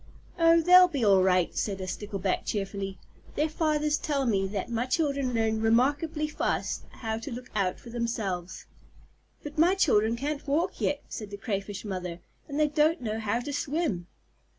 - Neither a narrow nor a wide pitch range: No, wide, 6.8 semitones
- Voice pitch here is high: Yes, high, 235 Hz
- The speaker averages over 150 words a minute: Yes, average, 175 wpm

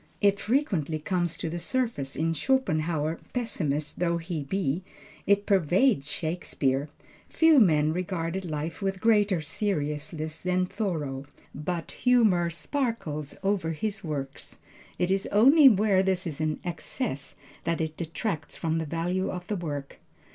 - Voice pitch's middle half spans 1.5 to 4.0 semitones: No, average, 4.5 semitones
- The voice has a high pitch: No, medium, 170 Hz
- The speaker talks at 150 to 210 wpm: No, average, 140 wpm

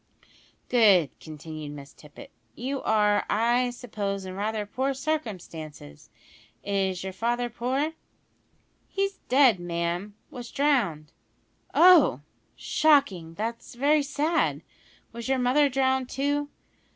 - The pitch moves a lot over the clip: Yes, wide, 6.5 semitones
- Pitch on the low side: No, high, 235 Hz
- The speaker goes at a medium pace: No, slow, 110 wpm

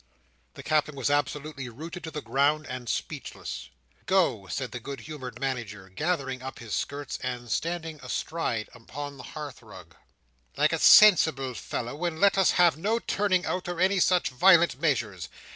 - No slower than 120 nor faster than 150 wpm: No, average, 165 wpm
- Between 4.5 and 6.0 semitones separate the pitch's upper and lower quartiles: Yes, average, 5.1 semitones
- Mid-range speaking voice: Yes, medium, 145 Hz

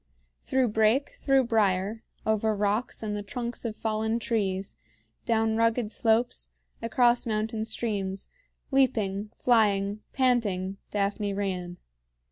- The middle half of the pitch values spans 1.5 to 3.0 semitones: Yes, narrow, 2.4 semitones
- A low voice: No, high, 220 Hz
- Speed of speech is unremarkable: No, slow, 110 wpm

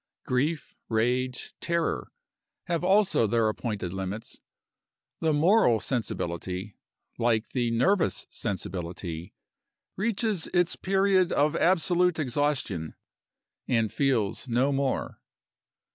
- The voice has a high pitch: No, low, 130 Hz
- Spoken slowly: Yes, slow, 95 wpm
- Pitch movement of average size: No, wide, 7.7 semitones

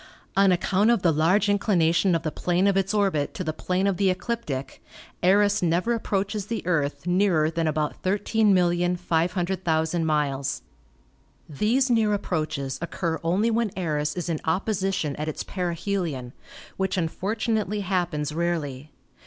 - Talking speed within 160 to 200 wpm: No, average, 145 wpm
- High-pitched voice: No, medium, 180 Hz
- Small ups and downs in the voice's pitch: No, average, 3.9 semitones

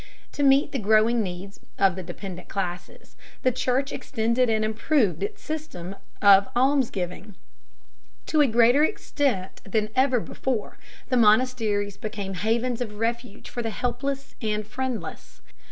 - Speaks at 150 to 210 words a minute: No, slow, 135 wpm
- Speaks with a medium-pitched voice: No, high, 225 Hz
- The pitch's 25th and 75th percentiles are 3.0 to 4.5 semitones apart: Yes, average, 4.1 semitones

